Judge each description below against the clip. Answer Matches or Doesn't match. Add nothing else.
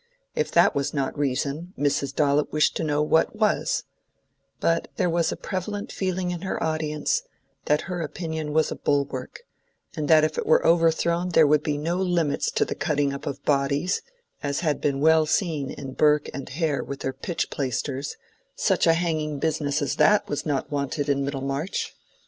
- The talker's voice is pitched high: Doesn't match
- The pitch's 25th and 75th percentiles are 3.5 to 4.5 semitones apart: Doesn't match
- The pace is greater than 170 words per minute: Matches